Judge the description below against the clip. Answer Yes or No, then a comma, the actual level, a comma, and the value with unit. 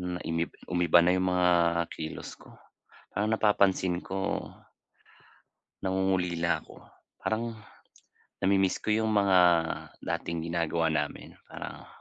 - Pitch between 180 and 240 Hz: No, very low, 95 Hz